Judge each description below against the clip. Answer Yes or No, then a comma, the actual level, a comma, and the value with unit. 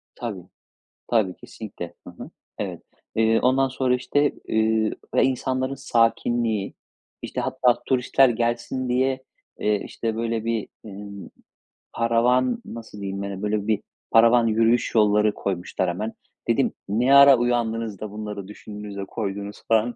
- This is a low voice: Yes, low, 115 Hz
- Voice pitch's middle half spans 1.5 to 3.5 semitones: Yes, average, 2.9 semitones